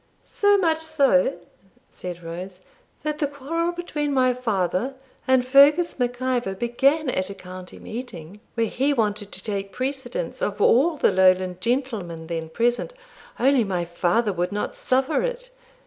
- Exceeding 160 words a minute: No, average, 150 wpm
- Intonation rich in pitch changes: Yes, wide, 7.1 semitones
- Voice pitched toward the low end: No, high, 245 Hz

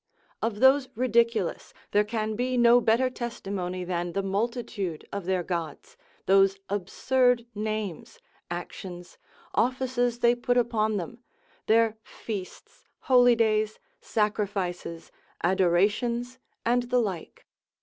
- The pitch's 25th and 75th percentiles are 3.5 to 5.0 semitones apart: Yes, average, 4.1 semitones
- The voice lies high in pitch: Yes, high, 215 Hz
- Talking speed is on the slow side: Yes, slow, 110 wpm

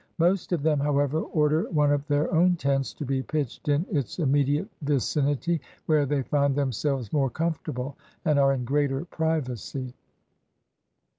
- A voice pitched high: No, medium, 145 Hz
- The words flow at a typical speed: Yes, average, 150 wpm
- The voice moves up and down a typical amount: No, narrow, 2.2 semitones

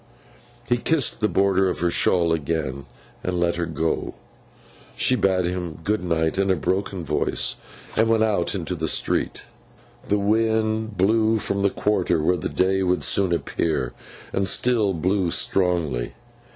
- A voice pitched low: Yes, very low, 95 Hz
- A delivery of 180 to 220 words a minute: No, average, 155 wpm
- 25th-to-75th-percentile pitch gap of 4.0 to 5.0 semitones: No, average, 3.6 semitones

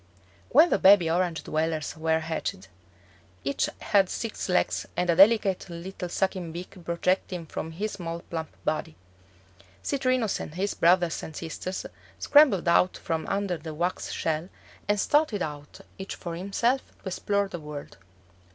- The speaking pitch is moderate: Yes, medium, 180 Hz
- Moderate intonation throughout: Yes, average, 3.5 semitones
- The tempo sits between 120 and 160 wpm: Yes, average, 150 wpm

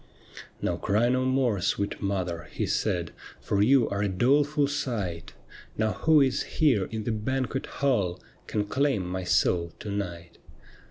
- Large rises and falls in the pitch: Yes, wide, 6.0 semitones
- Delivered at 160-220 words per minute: Yes, average, 165 wpm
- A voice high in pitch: No, low, 105 Hz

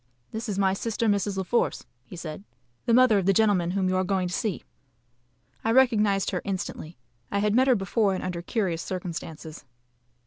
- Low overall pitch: No, high, 195 Hz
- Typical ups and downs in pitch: Yes, average, 3.0 semitones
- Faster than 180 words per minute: Yes, average, 195 wpm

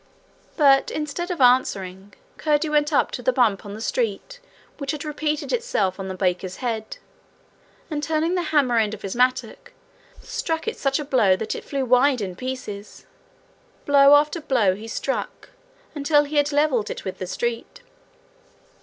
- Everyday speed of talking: Yes, average, 170 wpm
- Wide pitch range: Yes, wide, 5.8 semitones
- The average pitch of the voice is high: Yes, very high, 270 Hz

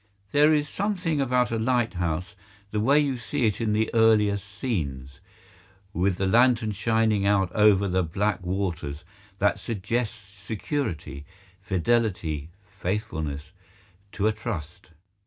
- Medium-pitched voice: No, low, 105 Hz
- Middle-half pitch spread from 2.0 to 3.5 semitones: No, average, 4.1 semitones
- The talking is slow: Yes, slow, 120 wpm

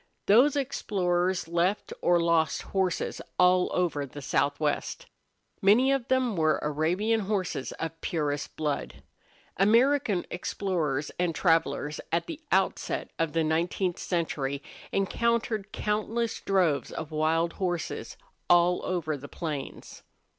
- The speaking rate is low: Yes, slow, 120 wpm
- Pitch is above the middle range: No, medium, 175 Hz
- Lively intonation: No, average, 4.3 semitones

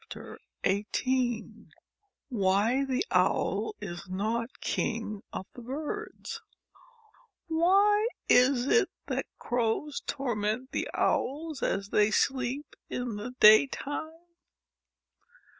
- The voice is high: Yes, very high, 250 Hz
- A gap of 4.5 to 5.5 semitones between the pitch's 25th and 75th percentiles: Yes, average, 5.1 semitones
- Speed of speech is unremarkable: No, slow, 95 wpm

